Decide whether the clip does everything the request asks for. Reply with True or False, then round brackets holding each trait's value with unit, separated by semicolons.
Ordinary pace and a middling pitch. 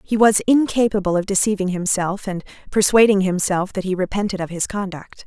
False (170 wpm; 195 Hz)